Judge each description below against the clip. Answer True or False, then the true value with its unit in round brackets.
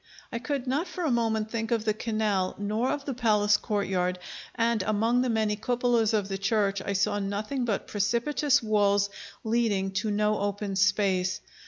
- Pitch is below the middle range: False (215 Hz)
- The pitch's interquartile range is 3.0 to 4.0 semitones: False (2.6 semitones)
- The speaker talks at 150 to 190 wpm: True (175 wpm)